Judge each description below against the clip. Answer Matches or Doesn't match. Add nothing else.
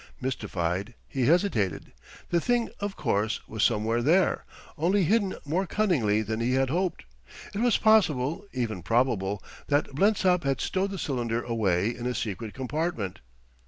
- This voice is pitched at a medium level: Doesn't match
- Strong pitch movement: Matches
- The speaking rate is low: Doesn't match